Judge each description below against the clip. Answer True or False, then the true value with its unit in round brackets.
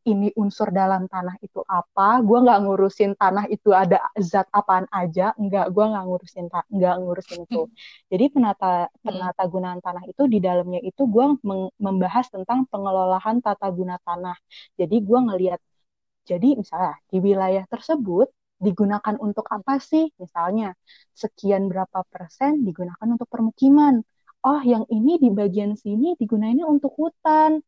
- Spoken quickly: True (145 wpm)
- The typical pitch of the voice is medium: False (205 Hz)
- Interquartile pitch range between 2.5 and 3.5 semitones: False (4.3 semitones)